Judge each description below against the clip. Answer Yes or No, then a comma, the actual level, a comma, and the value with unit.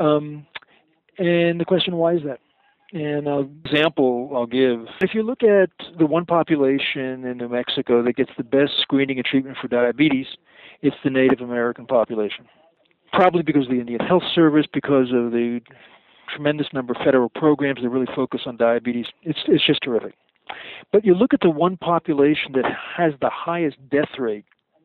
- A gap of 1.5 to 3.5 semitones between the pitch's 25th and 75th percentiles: No, average, 4.3 semitones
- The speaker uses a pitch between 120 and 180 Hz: Yes, medium, 140 Hz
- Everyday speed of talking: Yes, average, 175 wpm